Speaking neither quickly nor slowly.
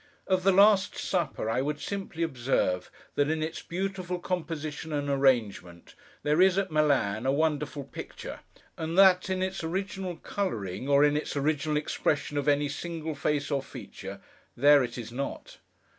Yes: average, 165 wpm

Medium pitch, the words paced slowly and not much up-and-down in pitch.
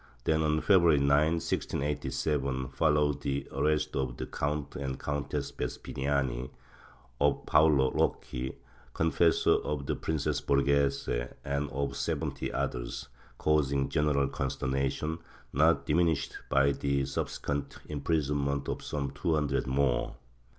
No: very low, 70 Hz; slow, 120 wpm; narrow, 1.7 semitones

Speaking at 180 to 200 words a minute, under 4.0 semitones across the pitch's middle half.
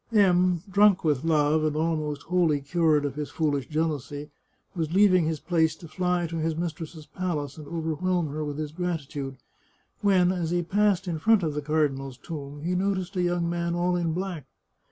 Yes: average, 190 wpm; average, 3.0 semitones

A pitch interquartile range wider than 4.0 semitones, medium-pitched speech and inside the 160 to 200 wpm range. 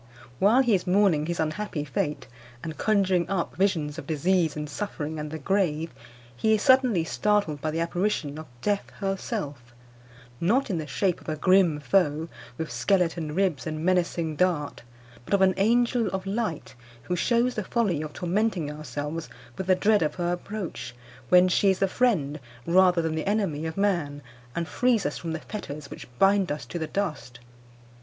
Yes: average, 4.4 semitones; medium, 175 Hz; average, 180 wpm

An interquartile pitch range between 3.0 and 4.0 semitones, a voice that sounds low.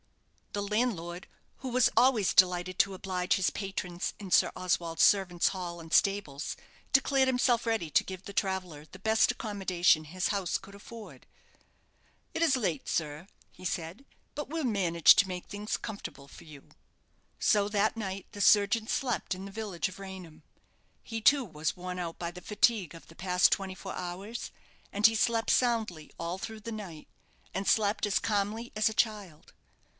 No: average, 3.6 semitones; high, 195 Hz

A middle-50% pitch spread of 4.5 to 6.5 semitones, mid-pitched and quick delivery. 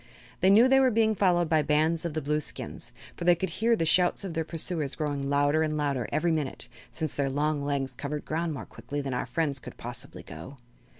No: average, 3.3 semitones; medium, 155 Hz; fast, 225 wpm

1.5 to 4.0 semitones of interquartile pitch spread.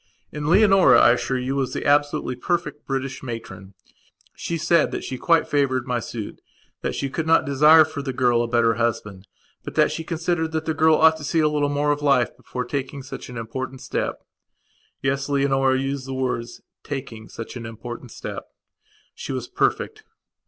Yes: average, 3.6 semitones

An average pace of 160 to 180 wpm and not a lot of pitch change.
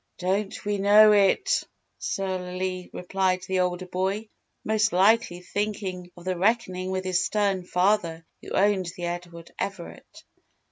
No: slow, 135 wpm; narrow, 2.2 semitones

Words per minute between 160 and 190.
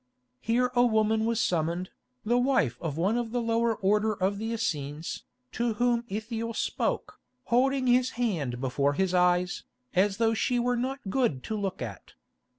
Yes: average, 165 wpm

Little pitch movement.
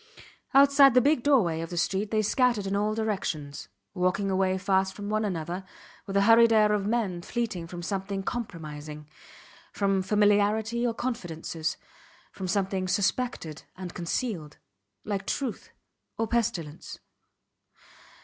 No: average, 3.9 semitones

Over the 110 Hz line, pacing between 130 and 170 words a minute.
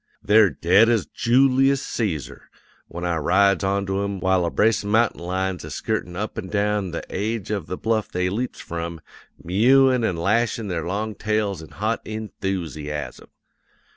No: low, 100 Hz; average, 165 wpm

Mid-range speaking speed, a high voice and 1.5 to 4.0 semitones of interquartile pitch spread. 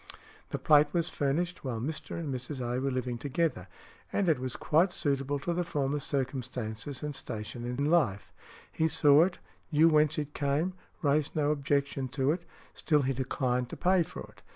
No: average, 180 wpm; medium, 140 Hz; average, 3.4 semitones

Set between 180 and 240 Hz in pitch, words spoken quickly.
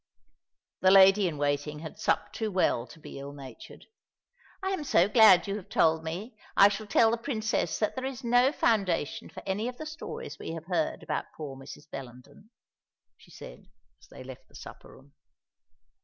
No: high, 190 Hz; average, 185 wpm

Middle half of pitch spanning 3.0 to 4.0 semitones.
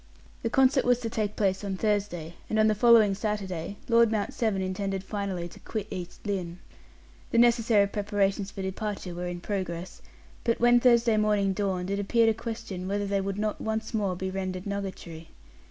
No: narrow, 2.5 semitones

